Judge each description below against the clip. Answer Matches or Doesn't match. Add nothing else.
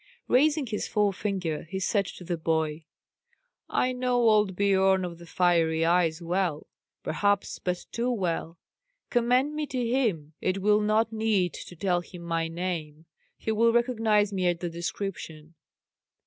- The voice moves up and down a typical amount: Matches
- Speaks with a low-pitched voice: Doesn't match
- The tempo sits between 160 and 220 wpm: Doesn't match